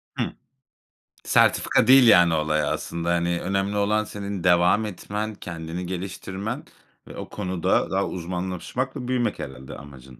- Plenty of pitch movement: No, average, 3.6 semitones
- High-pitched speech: No, very low, 90 Hz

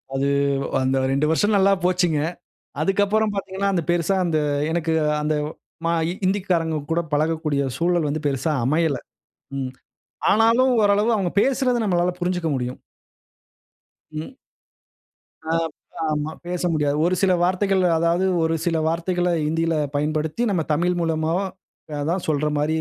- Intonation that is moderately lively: Yes, average, 3.4 semitones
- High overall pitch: No, medium, 170 Hz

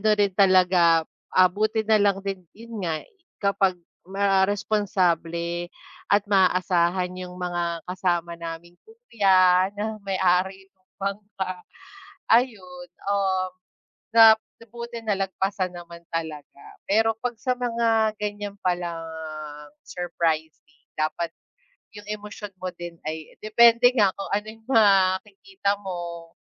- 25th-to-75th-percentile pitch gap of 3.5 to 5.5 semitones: No, average, 3.1 semitones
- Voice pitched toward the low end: No, high, 190 Hz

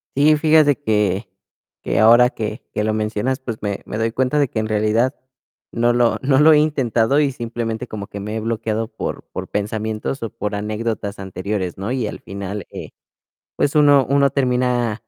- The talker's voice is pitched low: Yes, low, 115 Hz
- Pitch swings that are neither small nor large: Yes, average, 3.7 semitones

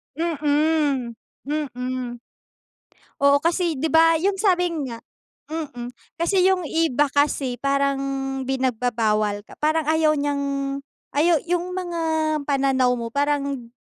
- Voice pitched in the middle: No, very high, 285 Hz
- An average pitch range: Yes, average, 4.0 semitones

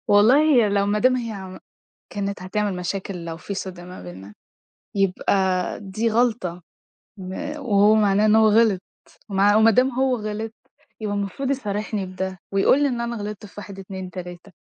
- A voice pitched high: Yes, high, 205 Hz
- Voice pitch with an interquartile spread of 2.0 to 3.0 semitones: Yes, average, 2.7 semitones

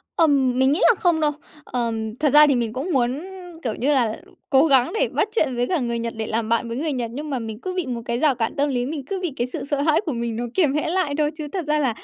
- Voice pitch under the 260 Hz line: No, very high, 265 Hz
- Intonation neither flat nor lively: Yes, average, 4.3 semitones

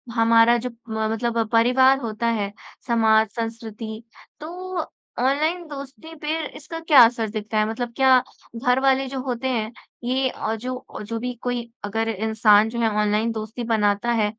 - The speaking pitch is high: Yes, high, 235 Hz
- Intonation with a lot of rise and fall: No, average, 2.9 semitones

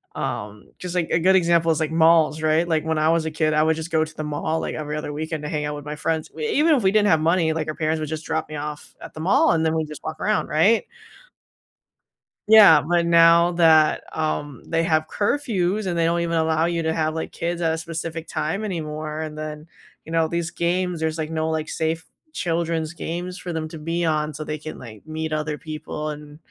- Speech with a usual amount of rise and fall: No, narrow, 1.5 semitones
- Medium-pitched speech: Yes, medium, 160 Hz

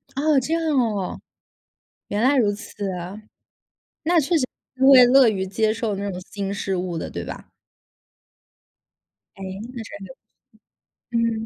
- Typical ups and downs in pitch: Yes, average, 4.7 semitones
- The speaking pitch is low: No, high, 215 Hz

